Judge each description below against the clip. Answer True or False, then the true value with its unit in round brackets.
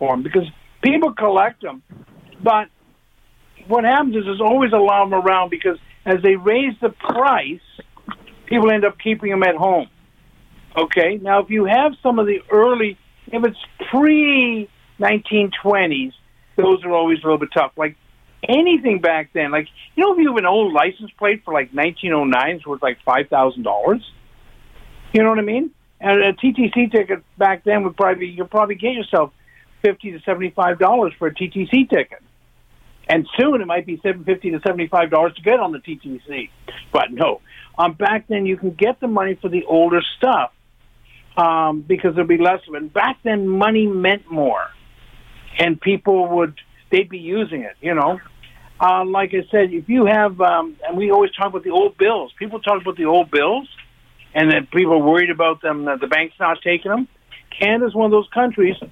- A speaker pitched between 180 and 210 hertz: True (190 Hz)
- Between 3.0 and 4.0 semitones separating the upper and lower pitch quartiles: False (4.4 semitones)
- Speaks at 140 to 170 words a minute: False (190 wpm)